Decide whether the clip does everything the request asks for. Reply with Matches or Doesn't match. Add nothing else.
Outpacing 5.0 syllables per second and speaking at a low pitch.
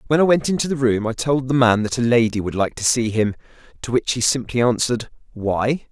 Matches